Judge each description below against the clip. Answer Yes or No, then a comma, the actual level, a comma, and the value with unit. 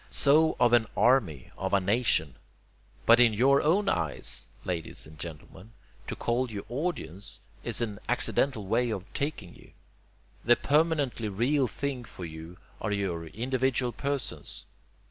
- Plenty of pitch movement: Yes, wide, 5.8 semitones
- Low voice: Yes, low, 115 Hz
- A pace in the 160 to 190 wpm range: No, average, 145 wpm